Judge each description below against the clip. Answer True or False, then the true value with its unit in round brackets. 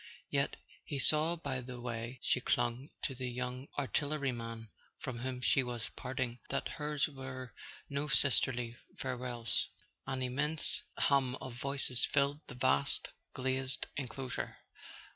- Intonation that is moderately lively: False (2.1 semitones)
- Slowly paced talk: True (130 wpm)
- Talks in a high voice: False (130 Hz)